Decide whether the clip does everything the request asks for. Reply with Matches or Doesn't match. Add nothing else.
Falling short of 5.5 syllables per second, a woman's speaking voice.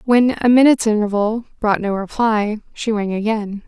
Matches